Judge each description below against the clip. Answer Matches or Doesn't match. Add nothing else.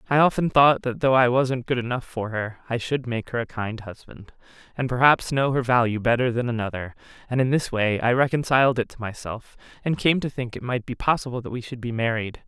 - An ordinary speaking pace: Doesn't match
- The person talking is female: Matches